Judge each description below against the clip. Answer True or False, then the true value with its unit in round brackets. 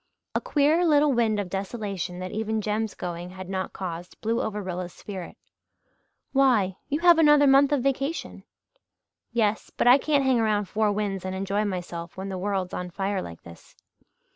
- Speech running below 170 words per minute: False (175 wpm)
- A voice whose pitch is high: True (205 Hz)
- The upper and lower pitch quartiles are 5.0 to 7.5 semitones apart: True (5.5 semitones)